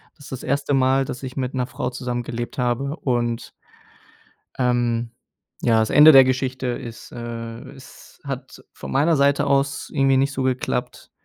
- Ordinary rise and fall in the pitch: No, narrow, 2.2 semitones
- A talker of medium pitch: No, low, 130 Hz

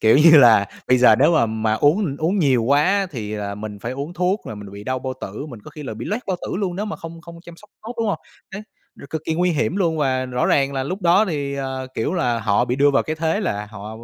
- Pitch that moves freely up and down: Yes, wide, 6.6 semitones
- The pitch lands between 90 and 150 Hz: Yes, medium, 140 Hz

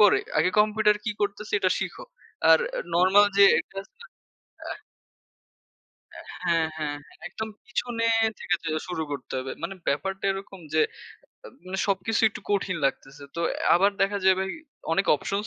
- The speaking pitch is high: Yes, high, 195 Hz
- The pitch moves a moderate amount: Yes, average, 3.6 semitones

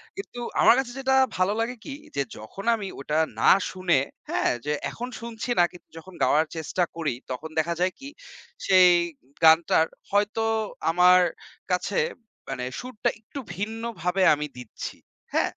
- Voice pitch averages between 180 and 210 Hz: Yes, medium, 185 Hz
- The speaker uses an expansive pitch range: Yes, wide, 5.9 semitones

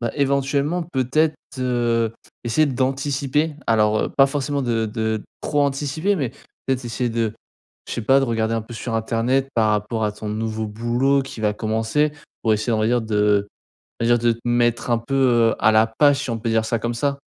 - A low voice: Yes, low, 120 Hz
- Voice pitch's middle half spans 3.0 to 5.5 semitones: Yes, average, 3.5 semitones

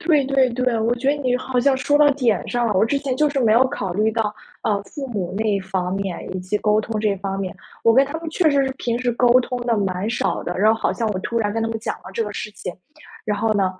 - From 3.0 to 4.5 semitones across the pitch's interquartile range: Yes, average, 4.2 semitones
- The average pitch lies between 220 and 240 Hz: Yes, high, 225 Hz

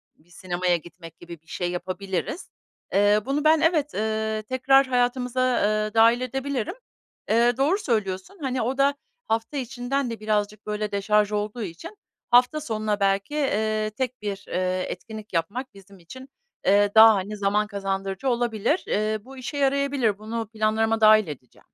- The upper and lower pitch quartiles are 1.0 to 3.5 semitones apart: No, average, 4.2 semitones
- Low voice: No, high, 215 Hz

